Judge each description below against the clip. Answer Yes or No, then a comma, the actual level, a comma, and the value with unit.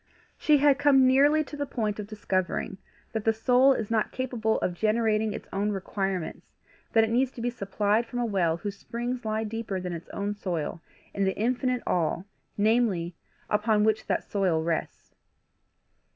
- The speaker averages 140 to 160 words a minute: No, average, 175 wpm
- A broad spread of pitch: No, average, 3.8 semitones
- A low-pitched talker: No, high, 215 Hz